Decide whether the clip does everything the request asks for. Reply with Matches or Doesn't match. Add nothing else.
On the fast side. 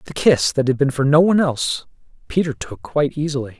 Matches